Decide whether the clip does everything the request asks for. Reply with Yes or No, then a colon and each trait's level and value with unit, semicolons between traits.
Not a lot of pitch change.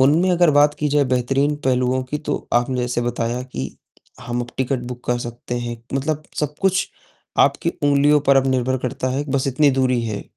No: average, 3.0 semitones